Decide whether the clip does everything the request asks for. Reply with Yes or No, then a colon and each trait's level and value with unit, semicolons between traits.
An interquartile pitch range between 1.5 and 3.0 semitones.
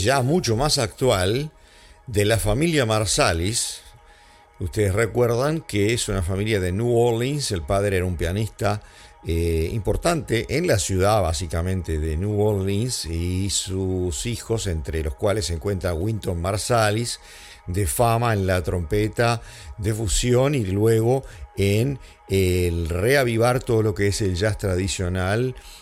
No: average, 4.0 semitones